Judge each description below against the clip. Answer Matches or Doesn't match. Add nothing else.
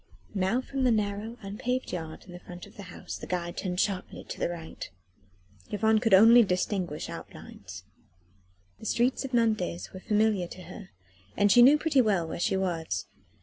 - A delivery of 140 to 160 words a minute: Doesn't match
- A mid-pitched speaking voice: Doesn't match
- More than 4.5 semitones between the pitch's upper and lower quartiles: Doesn't match